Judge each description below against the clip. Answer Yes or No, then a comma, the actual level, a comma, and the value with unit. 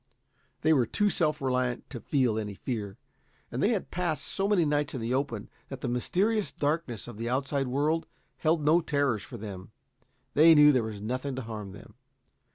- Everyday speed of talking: Yes, average, 190 wpm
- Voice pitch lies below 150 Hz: Yes, low, 135 Hz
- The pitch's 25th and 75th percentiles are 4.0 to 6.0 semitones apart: Yes, average, 5.0 semitones